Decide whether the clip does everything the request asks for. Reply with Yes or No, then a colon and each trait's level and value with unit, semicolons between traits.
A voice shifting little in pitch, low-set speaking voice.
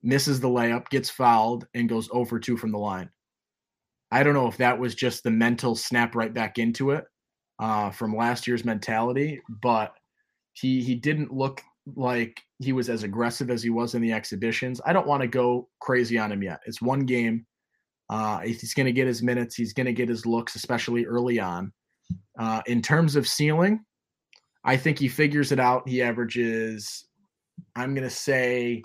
Yes: narrow, 2.2 semitones; low, 120 Hz